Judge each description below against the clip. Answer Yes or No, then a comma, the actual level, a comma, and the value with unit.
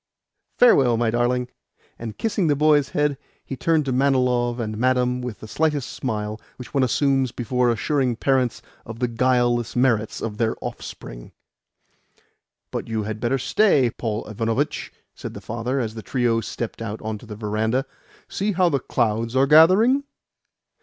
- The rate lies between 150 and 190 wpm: Yes, average, 160 wpm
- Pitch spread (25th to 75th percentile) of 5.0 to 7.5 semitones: No, average, 3.2 semitones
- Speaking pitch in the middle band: No, low, 125 Hz